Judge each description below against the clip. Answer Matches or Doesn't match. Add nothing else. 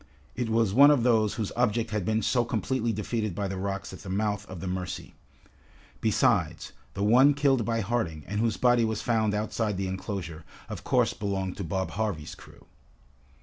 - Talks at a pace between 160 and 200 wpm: Matches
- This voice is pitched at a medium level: Doesn't match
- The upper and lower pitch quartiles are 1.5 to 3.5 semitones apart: Matches